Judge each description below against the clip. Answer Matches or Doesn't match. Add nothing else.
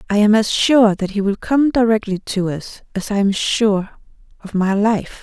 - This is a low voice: Doesn't match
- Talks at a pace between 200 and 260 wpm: Matches